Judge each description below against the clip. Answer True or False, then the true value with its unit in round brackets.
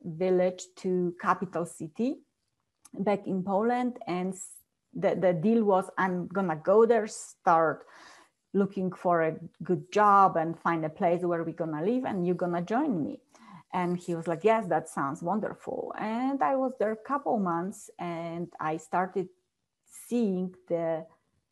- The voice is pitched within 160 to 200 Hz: True (185 Hz)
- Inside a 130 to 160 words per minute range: True (155 wpm)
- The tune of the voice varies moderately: True (4.1 semitones)